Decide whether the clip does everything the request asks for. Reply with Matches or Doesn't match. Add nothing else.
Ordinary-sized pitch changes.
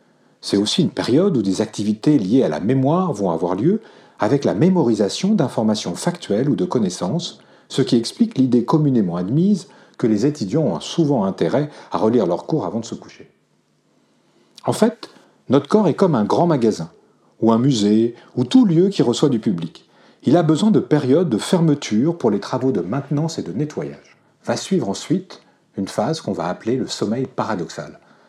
Doesn't match